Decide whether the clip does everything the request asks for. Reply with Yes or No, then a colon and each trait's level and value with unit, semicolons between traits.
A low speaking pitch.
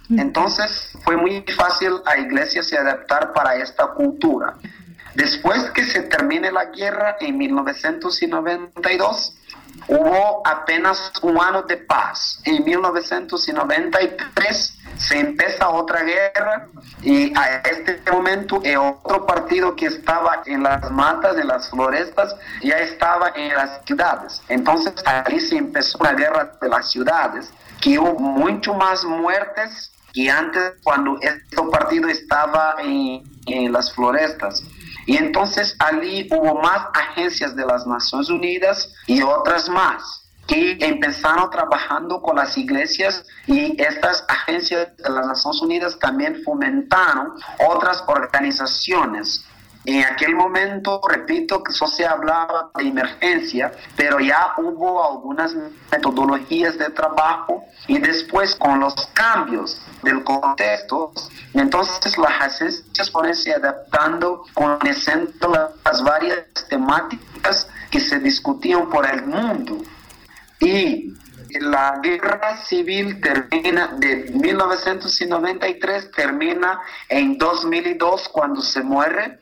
No: high, 190 Hz